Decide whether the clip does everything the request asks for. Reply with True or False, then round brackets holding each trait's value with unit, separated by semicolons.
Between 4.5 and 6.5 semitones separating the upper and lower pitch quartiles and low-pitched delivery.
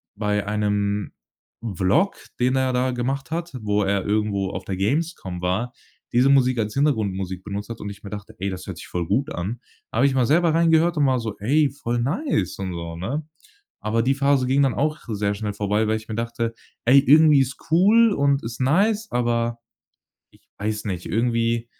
True (5.2 semitones; 115 Hz)